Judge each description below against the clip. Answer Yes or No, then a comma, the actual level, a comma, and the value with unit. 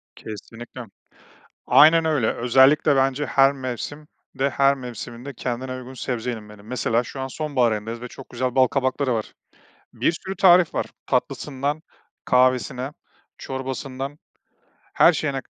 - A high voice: No, low, 130 Hz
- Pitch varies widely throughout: No, narrow, 2.4 semitones